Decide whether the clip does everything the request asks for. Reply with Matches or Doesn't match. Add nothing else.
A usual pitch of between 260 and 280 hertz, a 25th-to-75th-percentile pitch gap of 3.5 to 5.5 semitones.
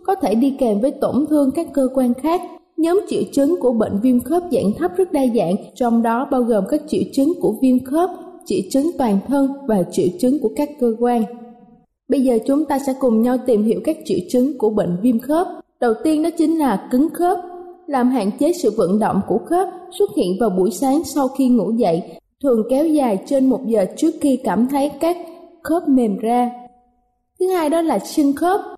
Matches